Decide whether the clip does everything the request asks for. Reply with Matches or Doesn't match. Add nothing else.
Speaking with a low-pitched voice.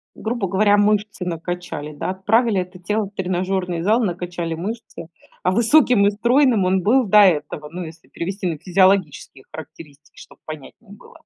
Doesn't match